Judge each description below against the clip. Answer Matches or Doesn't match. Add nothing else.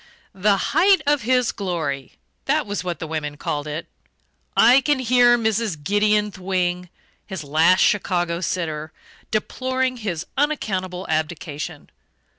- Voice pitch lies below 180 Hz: Doesn't match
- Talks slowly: Matches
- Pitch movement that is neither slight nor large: Doesn't match